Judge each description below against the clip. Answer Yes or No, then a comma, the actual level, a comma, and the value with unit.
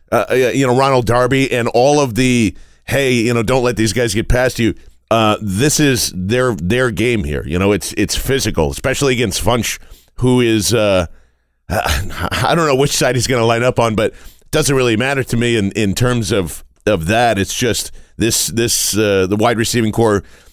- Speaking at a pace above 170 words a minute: Yes, fast, 205 wpm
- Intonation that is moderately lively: Yes, average, 4.0 semitones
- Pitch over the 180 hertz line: No, low, 115 Hz